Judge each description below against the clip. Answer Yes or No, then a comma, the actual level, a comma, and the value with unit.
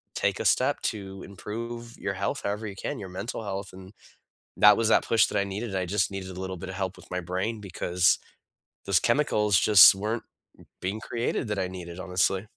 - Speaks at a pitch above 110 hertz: No, low, 100 Hz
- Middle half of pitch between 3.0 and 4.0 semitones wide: No, narrow, 2.4 semitones